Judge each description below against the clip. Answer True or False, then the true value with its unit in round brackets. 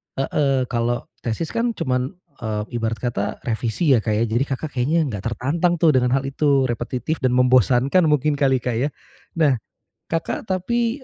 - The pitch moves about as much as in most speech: True (4.4 semitones)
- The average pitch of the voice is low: True (130 Hz)